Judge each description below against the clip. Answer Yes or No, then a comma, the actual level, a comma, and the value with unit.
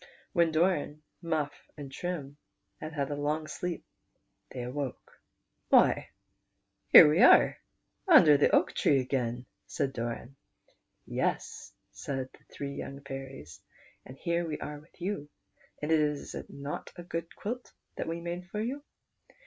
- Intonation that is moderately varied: Yes, average, 3.7 semitones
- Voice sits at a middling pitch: Yes, medium, 150 Hz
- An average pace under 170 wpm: Yes, average, 150 wpm